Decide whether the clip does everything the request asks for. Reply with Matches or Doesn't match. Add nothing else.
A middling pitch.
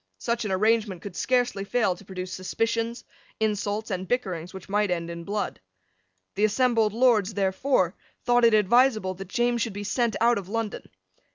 Doesn't match